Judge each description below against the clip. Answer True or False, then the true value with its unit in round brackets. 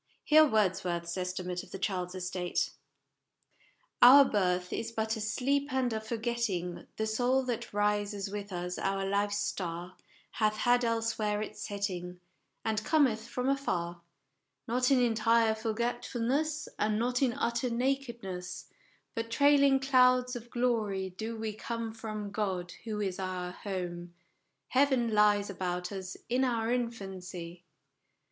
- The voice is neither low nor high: False (220 Hz)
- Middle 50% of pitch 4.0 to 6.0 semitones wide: True (4.4 semitones)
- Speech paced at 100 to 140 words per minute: True (135 wpm)